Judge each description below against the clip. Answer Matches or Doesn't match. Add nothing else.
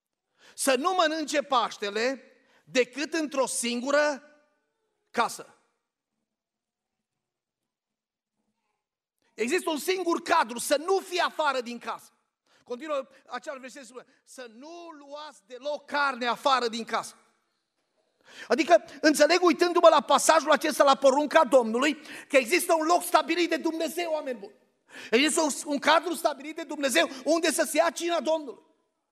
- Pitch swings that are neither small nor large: Matches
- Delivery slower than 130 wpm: Matches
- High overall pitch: Matches